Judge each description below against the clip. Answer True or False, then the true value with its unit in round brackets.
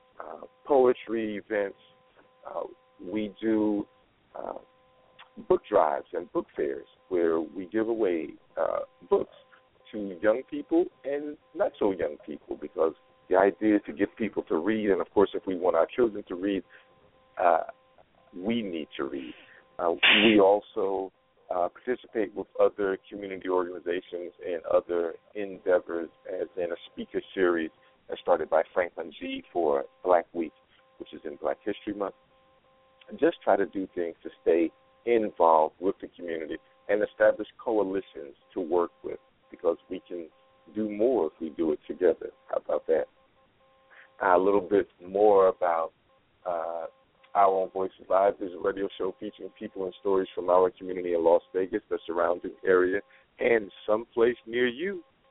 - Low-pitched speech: True (115 Hz)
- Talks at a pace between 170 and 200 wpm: False (155 wpm)